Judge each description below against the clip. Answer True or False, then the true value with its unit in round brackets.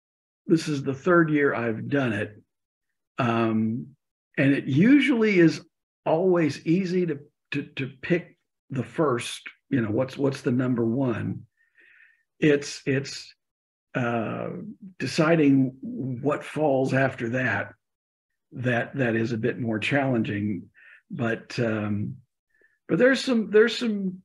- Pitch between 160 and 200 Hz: False (140 Hz)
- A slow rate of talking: True (125 wpm)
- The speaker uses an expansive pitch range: True (6.5 semitones)